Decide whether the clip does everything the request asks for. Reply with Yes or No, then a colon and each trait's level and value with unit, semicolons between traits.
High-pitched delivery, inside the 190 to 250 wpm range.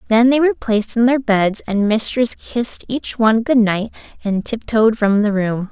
Yes: high, 225 Hz; average, 200 wpm